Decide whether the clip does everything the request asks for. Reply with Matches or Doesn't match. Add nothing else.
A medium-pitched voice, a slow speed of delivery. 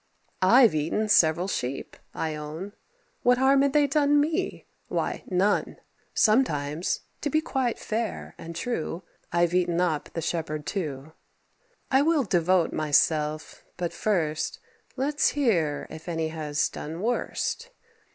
Matches